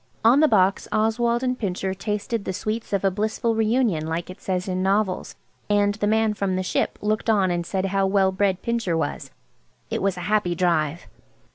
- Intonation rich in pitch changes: No, average, 2.9 semitones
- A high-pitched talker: Yes, high, 200 Hz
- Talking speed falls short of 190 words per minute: No, fast, 205 wpm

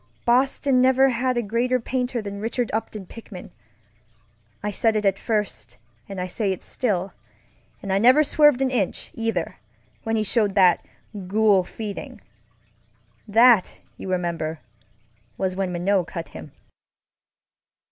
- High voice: Yes, high, 210 Hz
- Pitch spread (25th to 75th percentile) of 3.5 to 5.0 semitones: Yes, average, 4.4 semitones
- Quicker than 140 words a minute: No, slow, 135 wpm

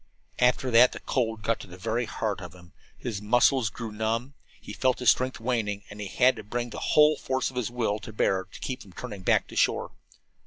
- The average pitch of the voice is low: Yes, low, 115 Hz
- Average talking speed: No, fast, 230 wpm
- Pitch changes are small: No, average, 3.3 semitones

